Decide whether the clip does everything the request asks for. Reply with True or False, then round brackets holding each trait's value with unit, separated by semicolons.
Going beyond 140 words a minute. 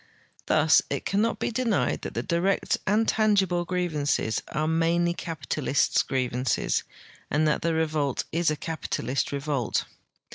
False (135 wpm)